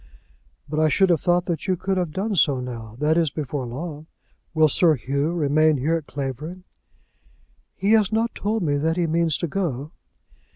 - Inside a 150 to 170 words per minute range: No, average, 190 wpm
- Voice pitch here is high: No, medium, 155 Hz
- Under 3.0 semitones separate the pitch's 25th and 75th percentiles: No, average, 3.7 semitones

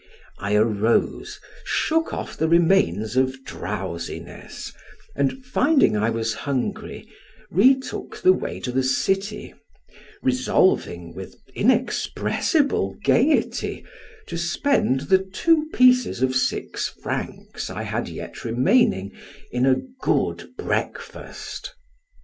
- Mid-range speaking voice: Yes, medium, 155 Hz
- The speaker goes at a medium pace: No, slow, 105 wpm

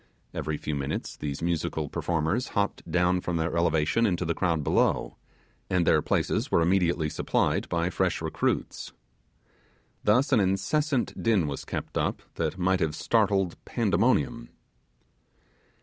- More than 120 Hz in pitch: No, very low, 90 Hz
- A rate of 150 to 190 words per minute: No, slow, 135 wpm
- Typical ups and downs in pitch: Yes, average, 3.9 semitones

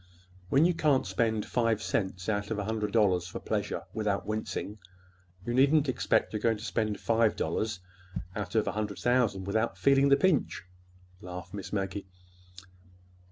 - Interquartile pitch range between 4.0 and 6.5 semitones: No, average, 2.9 semitones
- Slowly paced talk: No, average, 160 wpm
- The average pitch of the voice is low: Yes, low, 110 Hz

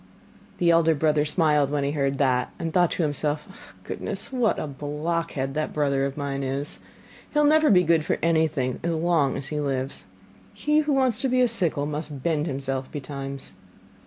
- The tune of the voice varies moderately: Yes, average, 3.4 semitones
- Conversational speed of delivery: Yes, average, 190 wpm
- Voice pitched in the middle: Yes, medium, 150 Hz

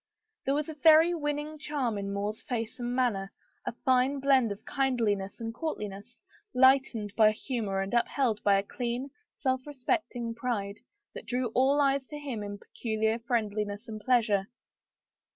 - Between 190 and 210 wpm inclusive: No, average, 160 wpm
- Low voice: No, high, 240 Hz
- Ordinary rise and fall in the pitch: Yes, average, 4.4 semitones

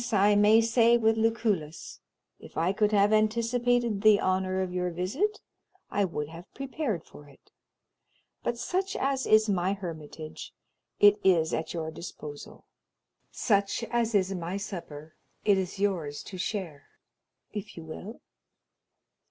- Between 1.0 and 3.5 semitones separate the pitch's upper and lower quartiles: No, average, 4.6 semitones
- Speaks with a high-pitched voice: Yes, high, 200 Hz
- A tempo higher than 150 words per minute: No, average, 140 wpm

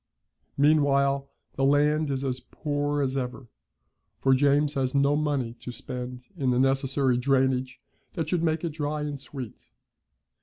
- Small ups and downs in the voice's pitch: Yes, narrow, 2.0 semitones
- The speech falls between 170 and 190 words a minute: No, average, 150 wpm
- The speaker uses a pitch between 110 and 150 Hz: Yes, medium, 140 Hz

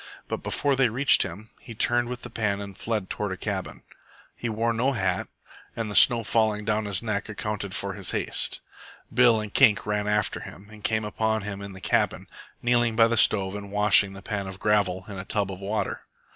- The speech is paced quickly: Yes, fast, 215 wpm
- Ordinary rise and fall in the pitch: No, narrow, 2.3 semitones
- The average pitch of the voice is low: Yes, low, 105 Hz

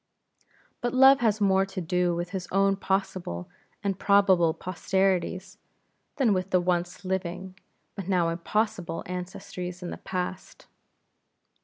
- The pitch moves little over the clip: Yes, narrow, 1.7 semitones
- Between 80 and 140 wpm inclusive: Yes, slow, 135 wpm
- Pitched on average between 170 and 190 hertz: Yes, medium, 185 Hz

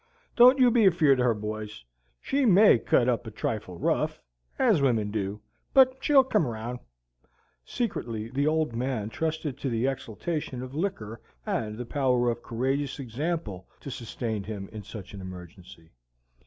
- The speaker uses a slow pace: No, average, 160 wpm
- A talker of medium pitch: No, low, 120 Hz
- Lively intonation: Yes, wide, 6.2 semitones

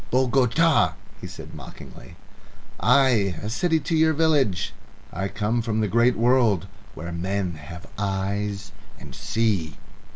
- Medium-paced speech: No, slow, 130 wpm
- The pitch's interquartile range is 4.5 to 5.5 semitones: Yes, average, 4.8 semitones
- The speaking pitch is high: No, low, 105 Hz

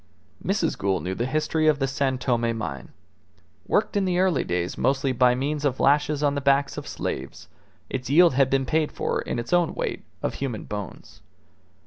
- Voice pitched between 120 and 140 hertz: Yes, low, 135 Hz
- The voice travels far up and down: No, average, 4.0 semitones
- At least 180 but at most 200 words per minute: Yes, average, 190 wpm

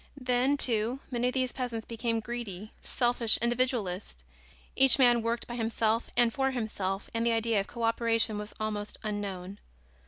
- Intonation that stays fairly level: Yes, narrow, 2.2 semitones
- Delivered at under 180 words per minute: Yes, average, 160 wpm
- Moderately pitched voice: No, high, 230 Hz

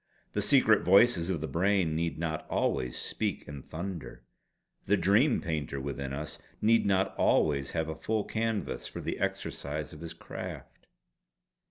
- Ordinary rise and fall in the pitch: Yes, average, 4.8 semitones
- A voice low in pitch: Yes, very low, 85 Hz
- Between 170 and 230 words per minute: No, average, 155 wpm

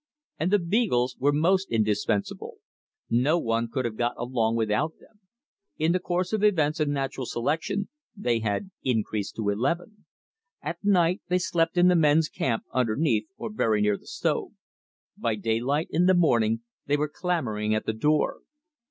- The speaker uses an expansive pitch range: Yes, wide, 7.3 semitones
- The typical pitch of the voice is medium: Yes, medium, 145 Hz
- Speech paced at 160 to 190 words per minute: Yes, average, 165 wpm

